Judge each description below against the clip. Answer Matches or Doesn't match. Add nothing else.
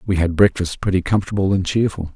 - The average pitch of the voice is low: Matches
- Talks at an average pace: Matches